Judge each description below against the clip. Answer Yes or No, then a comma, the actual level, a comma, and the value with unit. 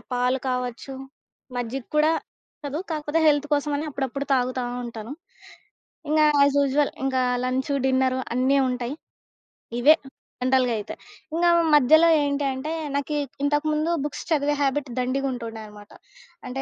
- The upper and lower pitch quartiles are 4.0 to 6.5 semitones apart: No, average, 2.7 semitones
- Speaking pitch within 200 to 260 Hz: No, very high, 270 Hz